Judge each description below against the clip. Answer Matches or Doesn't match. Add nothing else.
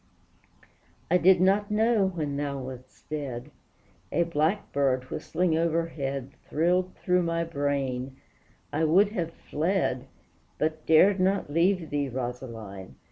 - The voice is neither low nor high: Matches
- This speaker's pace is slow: Matches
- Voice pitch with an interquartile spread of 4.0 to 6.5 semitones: Matches